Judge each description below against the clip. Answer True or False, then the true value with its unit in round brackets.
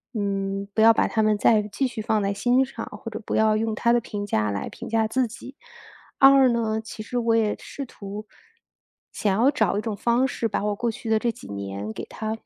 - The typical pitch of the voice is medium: False (220 Hz)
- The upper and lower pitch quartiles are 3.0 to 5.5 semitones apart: False (2.4 semitones)